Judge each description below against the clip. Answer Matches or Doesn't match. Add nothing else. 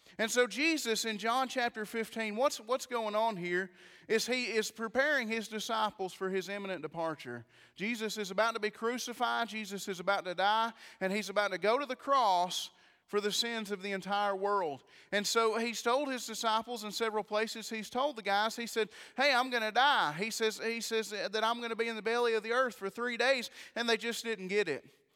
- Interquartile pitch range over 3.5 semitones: Doesn't match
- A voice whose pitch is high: Matches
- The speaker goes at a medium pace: Doesn't match